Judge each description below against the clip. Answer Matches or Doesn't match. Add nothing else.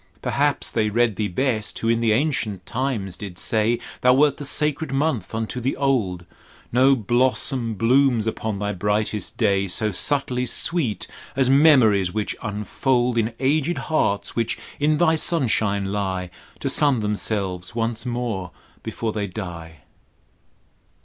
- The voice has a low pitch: Matches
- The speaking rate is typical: Matches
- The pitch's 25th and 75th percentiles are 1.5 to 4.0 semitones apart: Doesn't match